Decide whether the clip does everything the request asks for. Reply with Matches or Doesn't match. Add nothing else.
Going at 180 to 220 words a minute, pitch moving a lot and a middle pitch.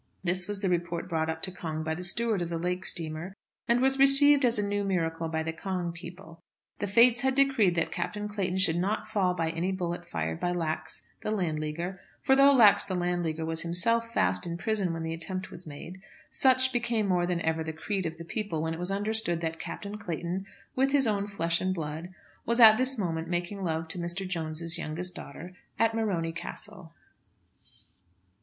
Doesn't match